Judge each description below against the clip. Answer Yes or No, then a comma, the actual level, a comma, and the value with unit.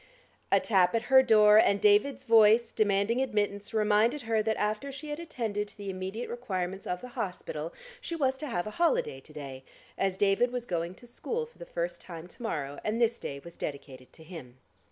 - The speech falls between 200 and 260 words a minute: Yes, fast, 205 wpm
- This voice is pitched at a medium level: No, high, 210 Hz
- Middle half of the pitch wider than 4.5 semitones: Yes, average, 5.1 semitones